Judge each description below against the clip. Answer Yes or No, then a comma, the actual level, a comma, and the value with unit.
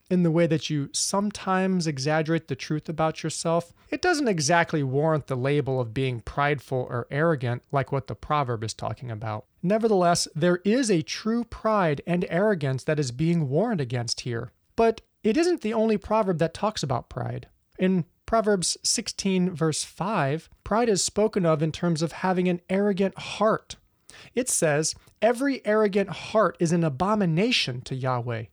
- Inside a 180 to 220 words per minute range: No, average, 165 wpm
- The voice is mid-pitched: Yes, medium, 165 Hz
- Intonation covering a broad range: Yes, wide, 6.3 semitones